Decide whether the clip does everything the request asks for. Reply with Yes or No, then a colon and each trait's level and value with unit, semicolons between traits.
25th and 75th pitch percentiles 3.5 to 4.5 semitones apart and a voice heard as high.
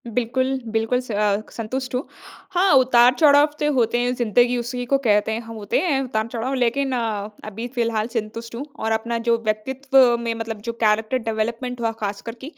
No: narrow, 2.5 semitones; high, 235 Hz